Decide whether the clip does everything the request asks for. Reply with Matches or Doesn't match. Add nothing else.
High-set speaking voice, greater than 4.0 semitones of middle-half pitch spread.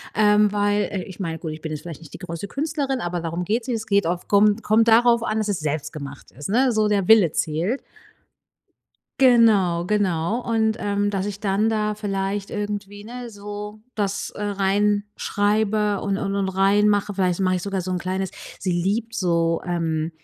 Doesn't match